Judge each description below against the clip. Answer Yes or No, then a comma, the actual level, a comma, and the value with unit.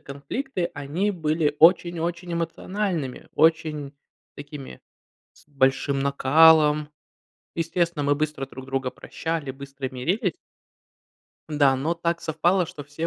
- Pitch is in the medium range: Yes, medium, 155 Hz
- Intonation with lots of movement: No, average, 3.3 semitones